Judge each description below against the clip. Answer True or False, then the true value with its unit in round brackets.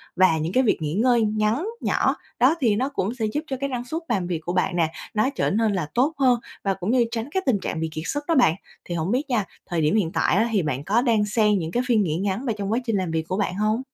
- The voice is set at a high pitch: True (215 Hz)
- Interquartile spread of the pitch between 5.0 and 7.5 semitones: True (5.3 semitones)